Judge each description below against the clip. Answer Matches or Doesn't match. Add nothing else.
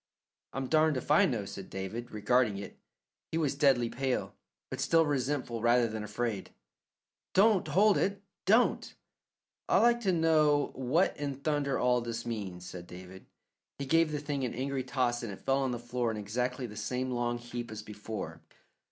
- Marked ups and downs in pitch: Doesn't match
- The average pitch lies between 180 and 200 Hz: Doesn't match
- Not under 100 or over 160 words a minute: Doesn't match